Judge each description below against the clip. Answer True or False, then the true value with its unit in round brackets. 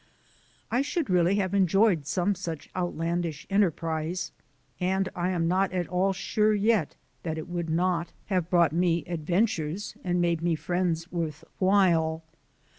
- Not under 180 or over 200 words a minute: False (145 wpm)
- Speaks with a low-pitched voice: False (175 Hz)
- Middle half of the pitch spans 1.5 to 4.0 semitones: True (2.4 semitones)